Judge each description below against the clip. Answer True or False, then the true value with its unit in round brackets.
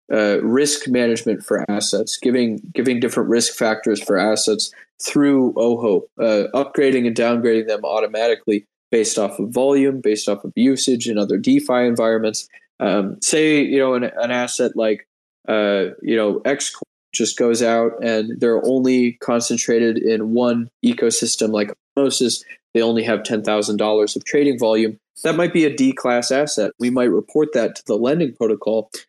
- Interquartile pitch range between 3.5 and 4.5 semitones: False (2.9 semitones)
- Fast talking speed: False (165 wpm)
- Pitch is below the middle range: True (120 Hz)